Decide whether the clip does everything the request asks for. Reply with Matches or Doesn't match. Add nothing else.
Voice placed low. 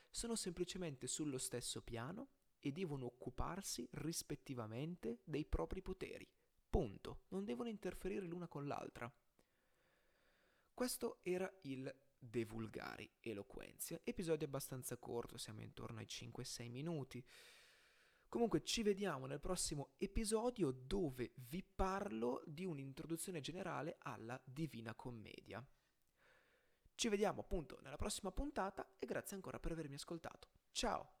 Doesn't match